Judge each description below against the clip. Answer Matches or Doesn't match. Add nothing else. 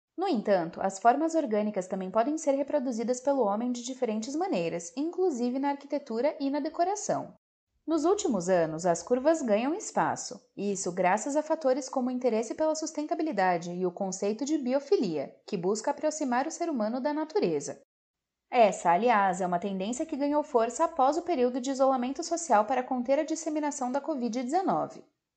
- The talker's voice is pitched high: Matches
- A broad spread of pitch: Matches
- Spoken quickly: Doesn't match